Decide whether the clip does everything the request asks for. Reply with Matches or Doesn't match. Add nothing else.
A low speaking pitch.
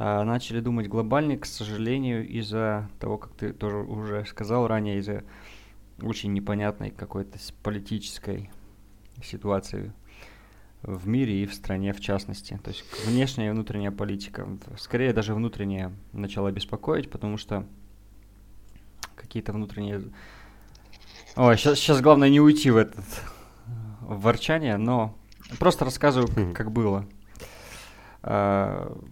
Matches